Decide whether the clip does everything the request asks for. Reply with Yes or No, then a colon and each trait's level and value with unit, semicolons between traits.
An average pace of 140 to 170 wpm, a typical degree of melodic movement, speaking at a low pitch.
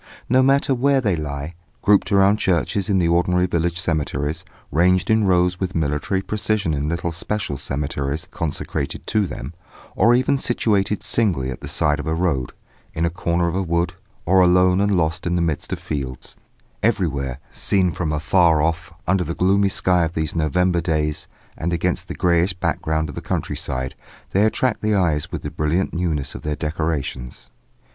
No: average, 180 wpm; average, 3.7 semitones; very low, 85 Hz